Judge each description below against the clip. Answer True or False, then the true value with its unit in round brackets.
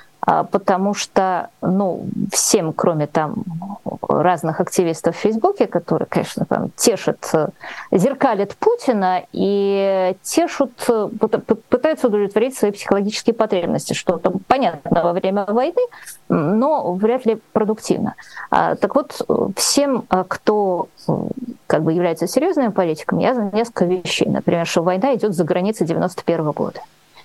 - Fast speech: False (115 wpm)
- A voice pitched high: True (200 Hz)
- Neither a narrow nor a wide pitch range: True (4.3 semitones)